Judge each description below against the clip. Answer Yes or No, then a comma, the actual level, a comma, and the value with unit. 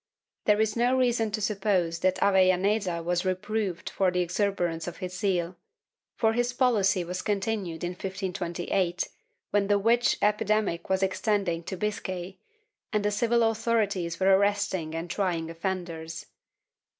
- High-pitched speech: Yes, high, 195 Hz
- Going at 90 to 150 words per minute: Yes, average, 140 wpm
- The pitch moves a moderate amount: Yes, average, 3.1 semitones